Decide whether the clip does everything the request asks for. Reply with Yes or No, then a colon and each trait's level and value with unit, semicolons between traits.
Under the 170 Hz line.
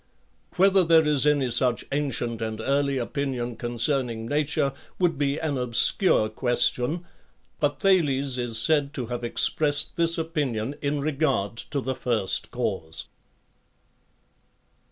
Yes: medium, 140 Hz